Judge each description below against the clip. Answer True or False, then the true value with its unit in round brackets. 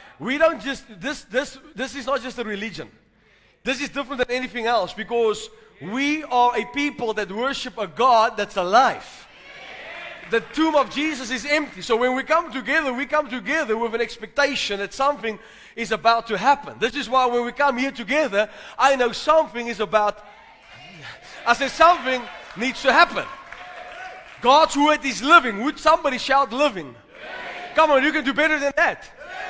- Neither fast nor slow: True (175 wpm)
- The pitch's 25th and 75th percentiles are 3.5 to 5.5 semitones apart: True (4.0 semitones)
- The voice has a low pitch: False (260 Hz)